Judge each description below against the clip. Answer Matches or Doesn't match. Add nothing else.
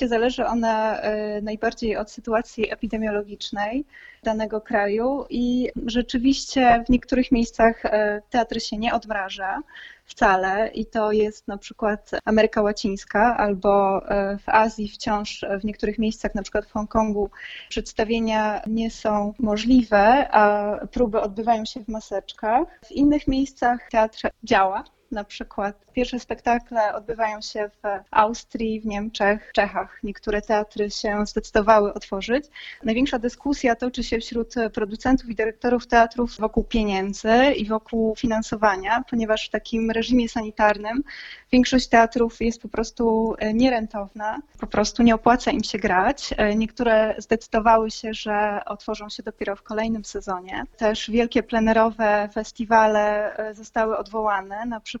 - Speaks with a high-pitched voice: Matches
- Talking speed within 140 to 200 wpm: Doesn't match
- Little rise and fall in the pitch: Matches